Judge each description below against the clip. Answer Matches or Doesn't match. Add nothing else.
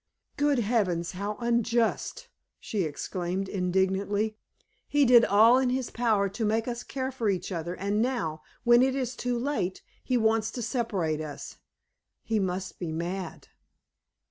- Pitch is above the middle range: Matches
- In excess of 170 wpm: Doesn't match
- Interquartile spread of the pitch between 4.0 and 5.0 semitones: Matches